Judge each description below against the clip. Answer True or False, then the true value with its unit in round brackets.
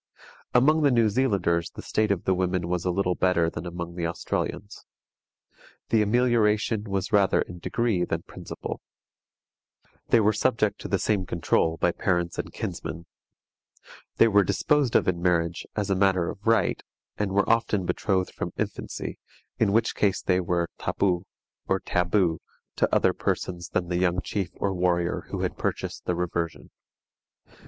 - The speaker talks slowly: False (160 wpm)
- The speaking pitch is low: True (95 Hz)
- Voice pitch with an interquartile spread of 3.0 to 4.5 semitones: True (3.3 semitones)